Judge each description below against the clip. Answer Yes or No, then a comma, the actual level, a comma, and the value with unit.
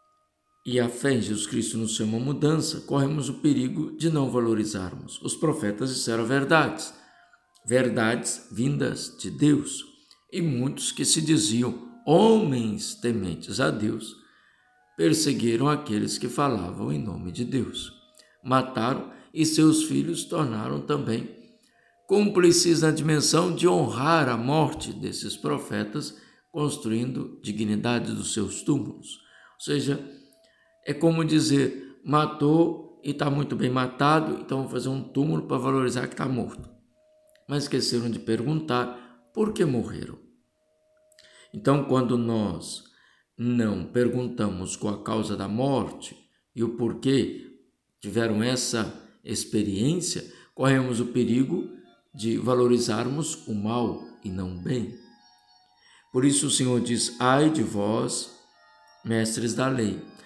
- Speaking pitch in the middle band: No, low, 125 Hz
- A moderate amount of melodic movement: Yes, average, 4.6 semitones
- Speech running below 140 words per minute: Yes, average, 125 wpm